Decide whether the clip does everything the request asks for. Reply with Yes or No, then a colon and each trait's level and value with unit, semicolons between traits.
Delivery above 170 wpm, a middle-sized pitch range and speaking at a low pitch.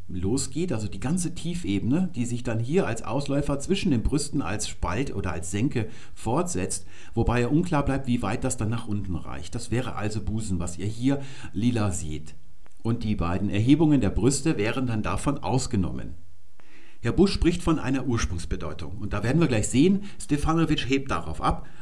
No: average, 180 wpm; wide, 6.4 semitones; low, 115 Hz